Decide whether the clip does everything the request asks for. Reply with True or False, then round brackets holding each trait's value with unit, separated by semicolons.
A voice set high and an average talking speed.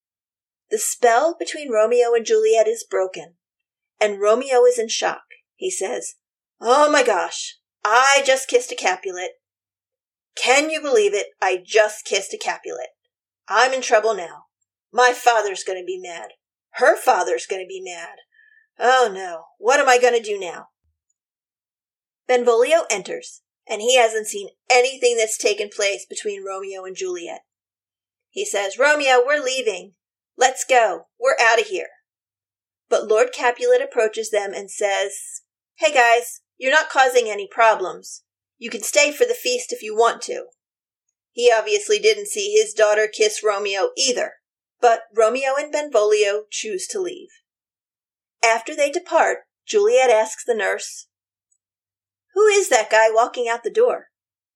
True (250 Hz; 150 wpm)